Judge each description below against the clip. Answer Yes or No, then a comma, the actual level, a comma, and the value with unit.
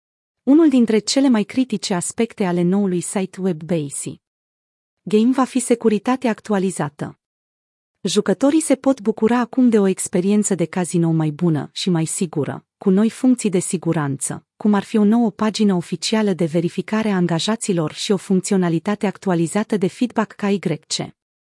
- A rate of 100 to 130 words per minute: No, average, 150 wpm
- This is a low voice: No, high, 195 Hz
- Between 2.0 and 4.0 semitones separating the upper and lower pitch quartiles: No, average, 4.4 semitones